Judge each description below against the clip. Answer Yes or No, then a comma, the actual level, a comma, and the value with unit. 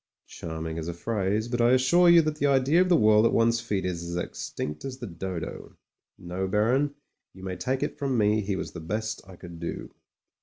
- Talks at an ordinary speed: No, fast, 220 wpm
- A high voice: No, low, 105 Hz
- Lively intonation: Yes, wide, 6.3 semitones